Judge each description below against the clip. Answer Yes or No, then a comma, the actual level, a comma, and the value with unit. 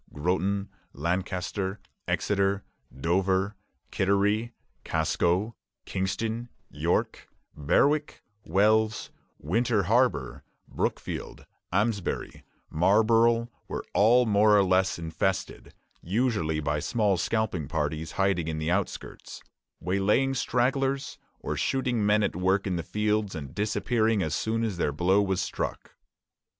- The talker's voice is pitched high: No, low, 100 Hz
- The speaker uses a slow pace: Yes, slow, 110 wpm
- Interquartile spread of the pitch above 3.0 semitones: Yes, average, 3.7 semitones